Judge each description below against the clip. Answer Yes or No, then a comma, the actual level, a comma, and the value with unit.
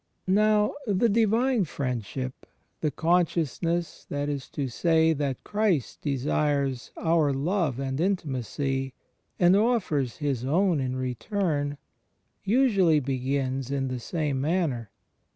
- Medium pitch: Yes, medium, 145 Hz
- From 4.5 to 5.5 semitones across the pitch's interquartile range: Yes, average, 5.2 semitones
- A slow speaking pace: Yes, slow, 120 wpm